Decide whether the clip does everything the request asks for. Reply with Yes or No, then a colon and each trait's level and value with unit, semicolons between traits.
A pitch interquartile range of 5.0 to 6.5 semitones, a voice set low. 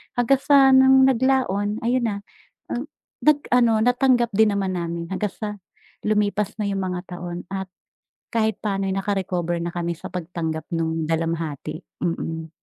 No: average, 5.3 semitones; high, 195 Hz